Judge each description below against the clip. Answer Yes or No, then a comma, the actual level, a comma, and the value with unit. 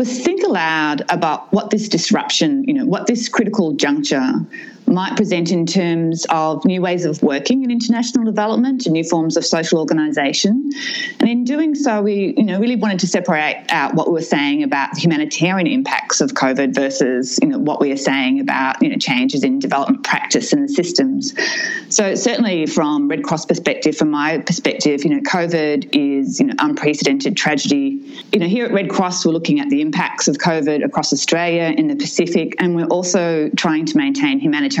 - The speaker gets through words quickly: No, average, 190 wpm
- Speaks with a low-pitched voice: No, high, 210 Hz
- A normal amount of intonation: No, wide, 8.8 semitones